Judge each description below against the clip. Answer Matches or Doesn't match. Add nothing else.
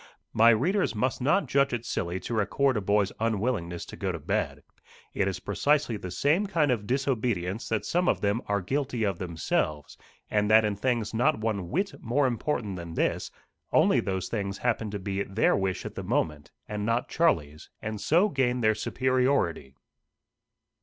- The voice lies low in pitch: Matches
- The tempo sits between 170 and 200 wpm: Matches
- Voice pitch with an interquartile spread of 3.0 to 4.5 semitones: Doesn't match